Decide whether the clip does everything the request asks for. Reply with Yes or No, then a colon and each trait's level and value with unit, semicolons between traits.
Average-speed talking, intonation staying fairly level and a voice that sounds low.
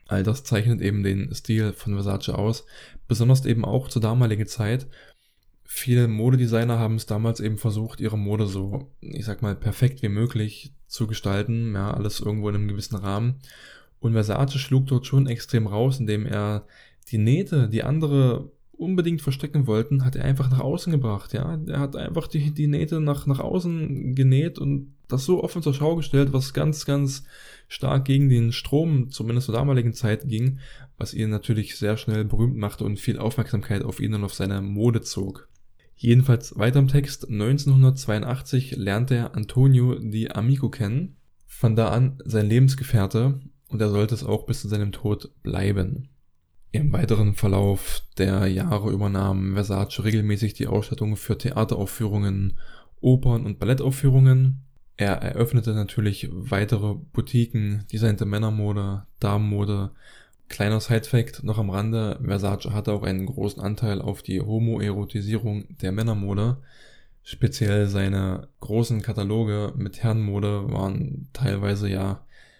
No: average, 150 wpm; average, 4.3 semitones; low, 115 Hz